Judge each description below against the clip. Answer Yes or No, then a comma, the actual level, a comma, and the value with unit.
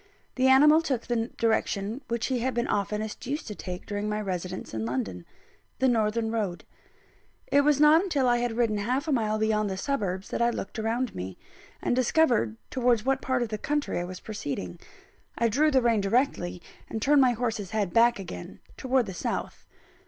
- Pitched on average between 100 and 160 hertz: No, high, 230 Hz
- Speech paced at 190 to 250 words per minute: Yes, average, 195 wpm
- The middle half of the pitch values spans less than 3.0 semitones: No, average, 4.3 semitones